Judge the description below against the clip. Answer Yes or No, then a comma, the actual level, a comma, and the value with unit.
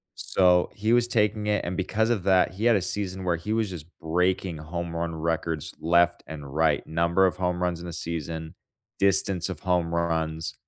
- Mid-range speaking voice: No, very low, 90 Hz